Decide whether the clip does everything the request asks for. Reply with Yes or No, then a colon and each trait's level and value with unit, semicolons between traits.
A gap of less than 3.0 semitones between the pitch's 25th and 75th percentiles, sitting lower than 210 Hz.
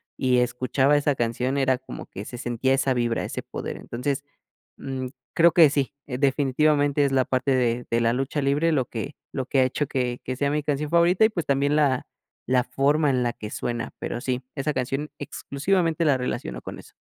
Yes: narrow, 2.6 semitones; low, 135 Hz